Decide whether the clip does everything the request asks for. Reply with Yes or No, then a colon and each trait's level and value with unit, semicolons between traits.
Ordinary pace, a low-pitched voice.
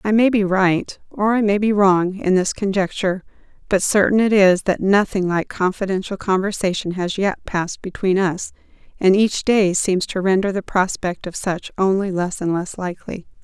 No: average, 185 wpm; high, 190 Hz